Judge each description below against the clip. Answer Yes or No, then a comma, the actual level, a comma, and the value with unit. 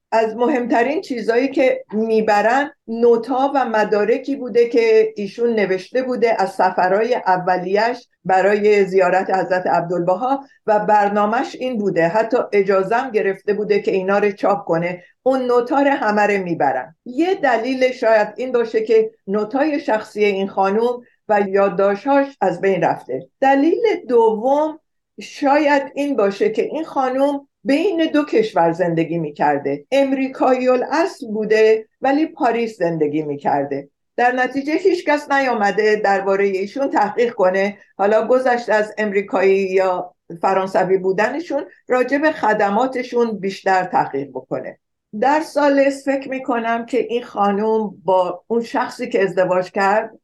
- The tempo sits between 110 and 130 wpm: Yes, average, 125 wpm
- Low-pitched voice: No, high, 220 Hz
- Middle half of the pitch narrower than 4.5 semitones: No, average, 5.2 semitones